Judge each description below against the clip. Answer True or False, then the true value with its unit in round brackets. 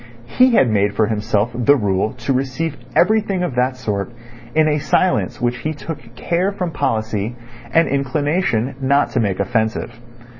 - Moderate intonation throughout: False (5.9 semitones)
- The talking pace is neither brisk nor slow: True (160 wpm)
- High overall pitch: False (130 Hz)